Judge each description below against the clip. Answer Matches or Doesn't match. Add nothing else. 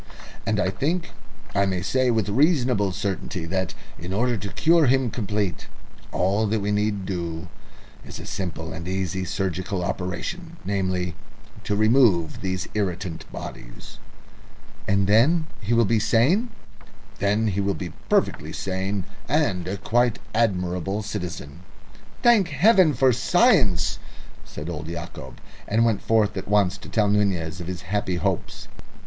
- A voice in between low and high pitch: Doesn't match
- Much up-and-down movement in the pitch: Doesn't match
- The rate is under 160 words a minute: Matches